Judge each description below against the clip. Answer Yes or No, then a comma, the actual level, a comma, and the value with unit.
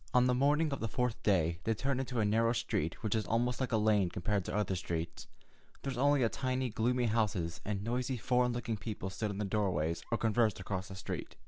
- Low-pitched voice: Yes, low, 110 Hz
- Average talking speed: No, fast, 225 wpm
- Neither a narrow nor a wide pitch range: Yes, average, 4.1 semitones